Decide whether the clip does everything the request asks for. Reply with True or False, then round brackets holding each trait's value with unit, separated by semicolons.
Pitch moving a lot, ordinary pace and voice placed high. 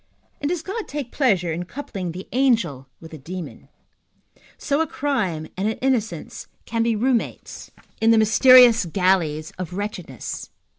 True (6.6 semitones; 155 wpm; 215 Hz)